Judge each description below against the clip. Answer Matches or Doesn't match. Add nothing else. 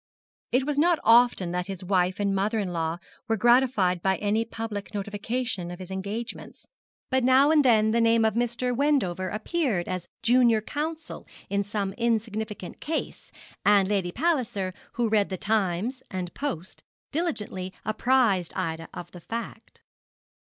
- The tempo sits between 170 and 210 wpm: Doesn't match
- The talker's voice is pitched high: Matches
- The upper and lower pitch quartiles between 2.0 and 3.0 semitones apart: Doesn't match